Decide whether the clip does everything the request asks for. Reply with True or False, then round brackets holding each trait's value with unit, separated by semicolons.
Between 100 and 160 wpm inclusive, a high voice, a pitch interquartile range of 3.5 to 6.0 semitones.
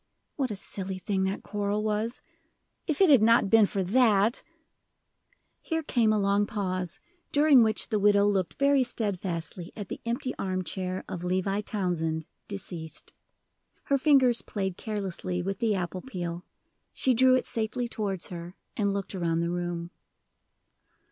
True (155 wpm; 200 Hz; 3.8 semitones)